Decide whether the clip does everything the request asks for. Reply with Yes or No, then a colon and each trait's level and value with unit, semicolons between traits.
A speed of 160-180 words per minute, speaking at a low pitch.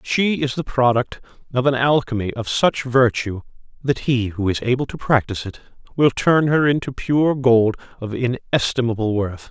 Yes: average, 170 wpm; low, 125 Hz